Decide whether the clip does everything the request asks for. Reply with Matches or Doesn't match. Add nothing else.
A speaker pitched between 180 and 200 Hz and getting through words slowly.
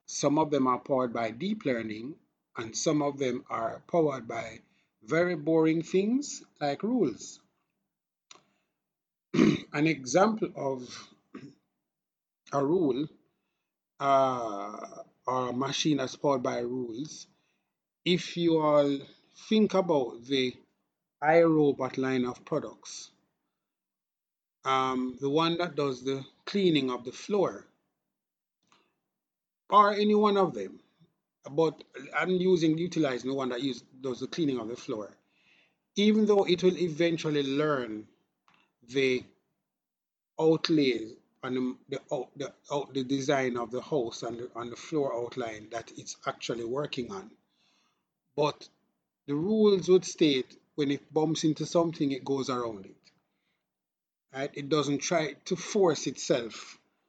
Doesn't match